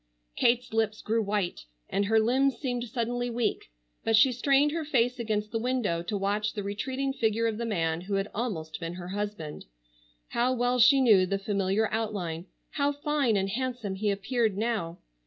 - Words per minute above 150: Yes, average, 180 wpm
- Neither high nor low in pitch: No, high, 220 Hz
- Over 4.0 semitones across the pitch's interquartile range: No, average, 3.7 semitones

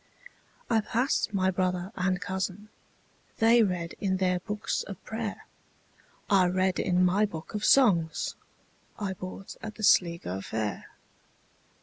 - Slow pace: Yes, slow, 115 wpm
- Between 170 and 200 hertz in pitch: Yes, high, 190 Hz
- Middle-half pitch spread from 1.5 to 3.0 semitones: Yes, average, 2.7 semitones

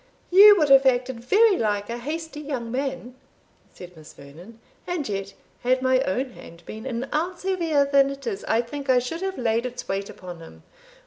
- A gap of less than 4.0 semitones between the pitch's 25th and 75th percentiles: No, average, 4.9 semitones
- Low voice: No, very high, 255 Hz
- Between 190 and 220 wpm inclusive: Yes, average, 195 wpm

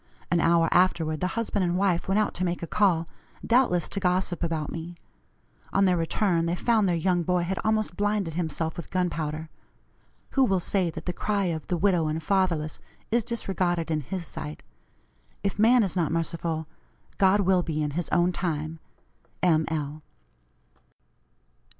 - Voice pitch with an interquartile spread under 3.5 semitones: Yes, average, 2.9 semitones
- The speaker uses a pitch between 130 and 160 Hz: No, medium, 175 Hz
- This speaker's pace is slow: No, average, 170 wpm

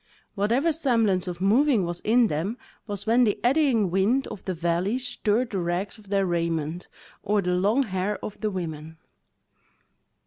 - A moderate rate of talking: Yes, average, 165 wpm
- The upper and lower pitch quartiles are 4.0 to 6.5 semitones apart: Yes, average, 4.5 semitones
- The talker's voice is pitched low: No, high, 200 Hz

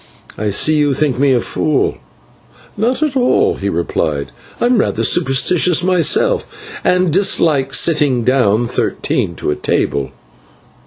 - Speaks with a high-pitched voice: No, medium, 150 Hz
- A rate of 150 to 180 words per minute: No, slow, 135 wpm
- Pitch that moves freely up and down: Yes, wide, 6.9 semitones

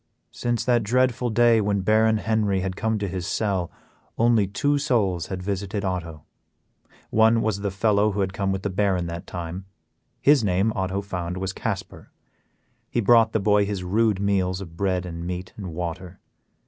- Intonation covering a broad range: No, average, 3.2 semitones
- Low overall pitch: Yes, low, 100 Hz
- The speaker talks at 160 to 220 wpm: Yes, average, 175 wpm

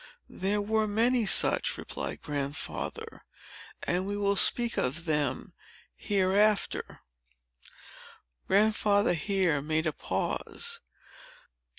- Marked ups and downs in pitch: No, average, 5.0 semitones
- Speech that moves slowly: Yes, slow, 100 wpm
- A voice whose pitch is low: No, high, 200 Hz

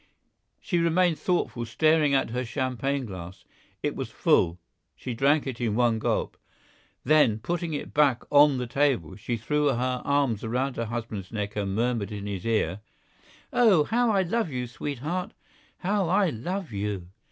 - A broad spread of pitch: Yes, wide, 5.7 semitones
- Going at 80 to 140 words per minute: No, average, 165 wpm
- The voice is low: Yes, low, 130 Hz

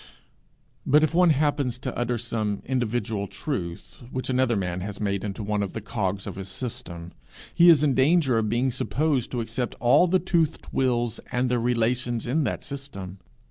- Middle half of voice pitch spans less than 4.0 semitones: No, average, 4.4 semitones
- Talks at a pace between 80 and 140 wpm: No, average, 180 wpm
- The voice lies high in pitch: No, low, 120 Hz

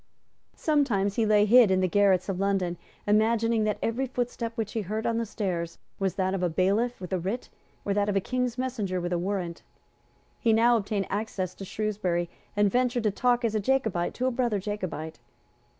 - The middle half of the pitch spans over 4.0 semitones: No, average, 3.6 semitones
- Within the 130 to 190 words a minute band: No, average, 200 wpm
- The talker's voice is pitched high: Yes, high, 205 Hz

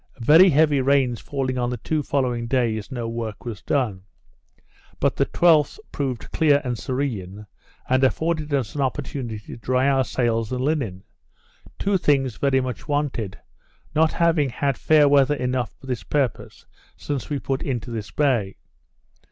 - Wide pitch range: No, average, 3.5 semitones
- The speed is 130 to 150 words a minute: No, average, 160 wpm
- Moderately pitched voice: No, low, 130 Hz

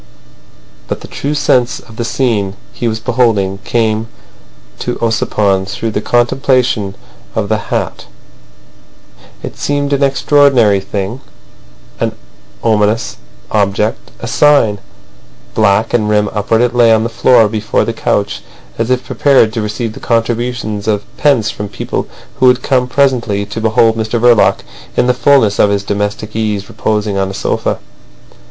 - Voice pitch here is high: No, low, 110 Hz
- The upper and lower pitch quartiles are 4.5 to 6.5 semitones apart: No, average, 2.9 semitones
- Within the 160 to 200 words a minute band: No, average, 150 wpm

